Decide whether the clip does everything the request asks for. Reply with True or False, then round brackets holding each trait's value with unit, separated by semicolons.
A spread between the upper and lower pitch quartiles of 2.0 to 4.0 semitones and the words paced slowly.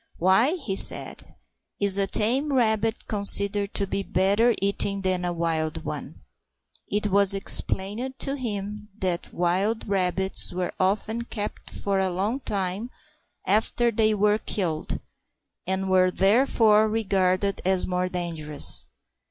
True (2.6 semitones; 130 wpm)